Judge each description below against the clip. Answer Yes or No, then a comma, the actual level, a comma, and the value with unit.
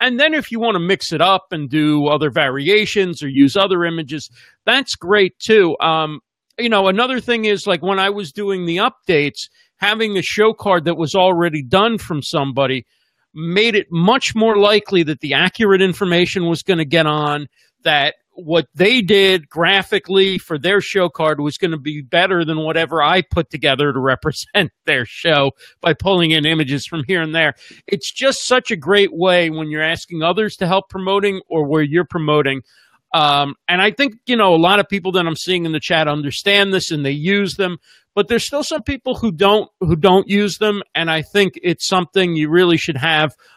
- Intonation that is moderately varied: Yes, average, 4.2 semitones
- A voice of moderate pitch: Yes, medium, 180 Hz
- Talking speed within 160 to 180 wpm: No, average, 200 wpm